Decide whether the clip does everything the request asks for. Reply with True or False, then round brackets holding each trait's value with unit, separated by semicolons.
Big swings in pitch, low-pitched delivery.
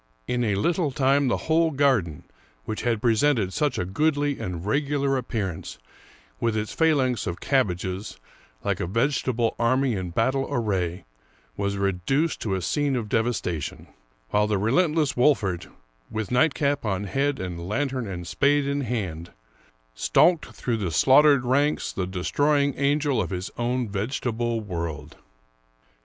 True (6.5 semitones; 120 Hz)